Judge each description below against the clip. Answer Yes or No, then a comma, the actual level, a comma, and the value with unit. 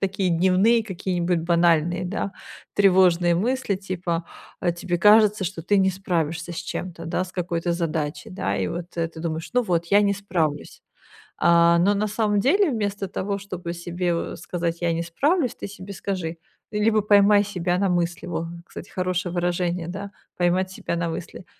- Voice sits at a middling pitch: Yes, medium, 180 Hz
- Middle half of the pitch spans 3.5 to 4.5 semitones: No, average, 2.8 semitones